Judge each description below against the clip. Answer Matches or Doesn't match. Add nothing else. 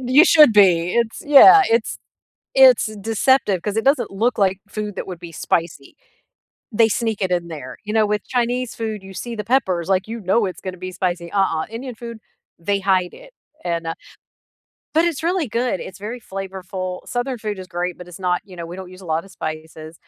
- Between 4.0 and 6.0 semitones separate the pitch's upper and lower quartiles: Matches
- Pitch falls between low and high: Doesn't match